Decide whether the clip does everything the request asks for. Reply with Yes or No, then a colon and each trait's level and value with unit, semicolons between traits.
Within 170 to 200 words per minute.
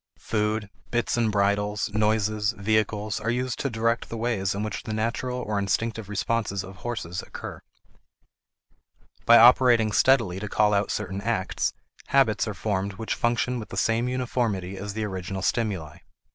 No: average, 160 wpm